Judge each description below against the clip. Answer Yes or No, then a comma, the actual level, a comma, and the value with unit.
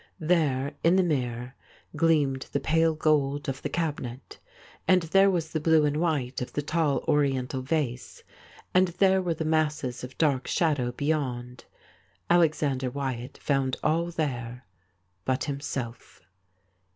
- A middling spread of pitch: Yes, average, 3.8 semitones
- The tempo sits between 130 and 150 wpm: Yes, average, 140 wpm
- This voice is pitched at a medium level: Yes, medium, 145 Hz